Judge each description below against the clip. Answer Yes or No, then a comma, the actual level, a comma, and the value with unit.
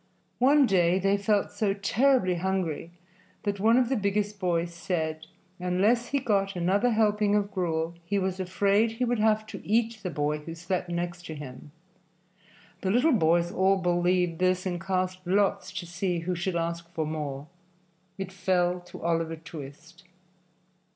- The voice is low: No, medium, 185 Hz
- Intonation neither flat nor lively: Yes, average, 3.2 semitones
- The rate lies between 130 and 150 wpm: No, average, 160 wpm